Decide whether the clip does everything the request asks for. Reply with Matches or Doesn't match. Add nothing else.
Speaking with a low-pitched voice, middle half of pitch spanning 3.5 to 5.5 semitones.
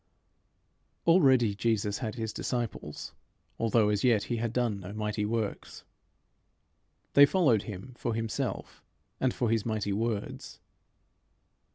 Doesn't match